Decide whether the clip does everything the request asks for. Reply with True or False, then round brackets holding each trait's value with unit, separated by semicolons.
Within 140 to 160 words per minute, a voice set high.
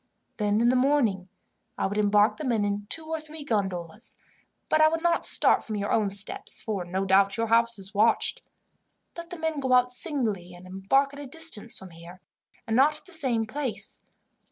False (205 wpm; 225 Hz)